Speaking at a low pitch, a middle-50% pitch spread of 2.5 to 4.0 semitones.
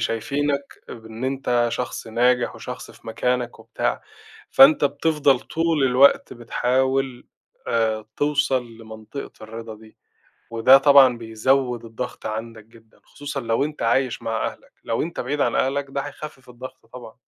Yes: low, 125 Hz; average, 3.4 semitones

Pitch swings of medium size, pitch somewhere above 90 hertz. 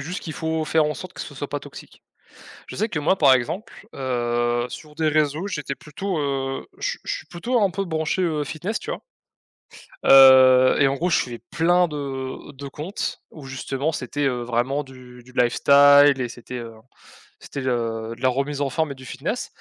Yes: average, 3.5 semitones; medium, 140 Hz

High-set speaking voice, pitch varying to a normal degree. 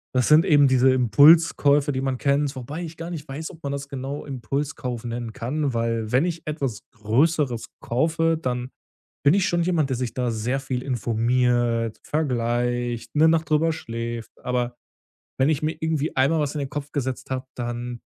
No: low, 135 Hz; average, 3.9 semitones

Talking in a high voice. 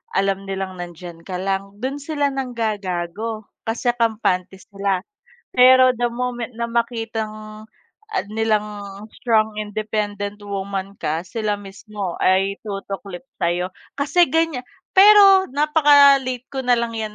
Yes: high, 215 Hz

